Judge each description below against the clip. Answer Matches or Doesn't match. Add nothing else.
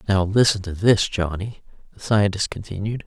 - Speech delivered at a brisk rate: Doesn't match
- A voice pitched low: Matches